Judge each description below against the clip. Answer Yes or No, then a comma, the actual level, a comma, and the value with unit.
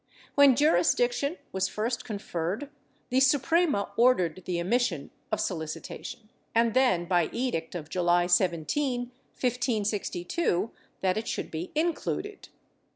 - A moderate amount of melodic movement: No, wide, 6.7 semitones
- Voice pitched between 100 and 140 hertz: No, high, 220 Hz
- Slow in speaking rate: Yes, slow, 120 wpm